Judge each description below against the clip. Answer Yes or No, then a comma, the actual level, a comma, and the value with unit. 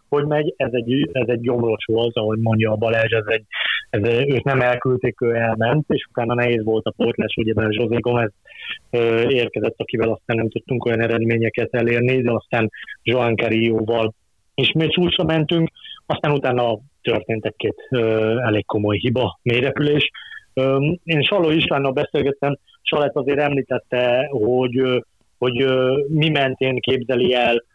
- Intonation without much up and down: No, average, 3.2 semitones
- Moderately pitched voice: No, low, 125 Hz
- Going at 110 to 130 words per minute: No, average, 150 wpm